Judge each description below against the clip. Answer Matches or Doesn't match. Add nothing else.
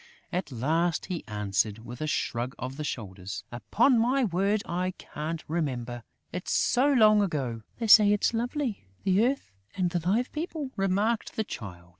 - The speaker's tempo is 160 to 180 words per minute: Matches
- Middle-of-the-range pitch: Matches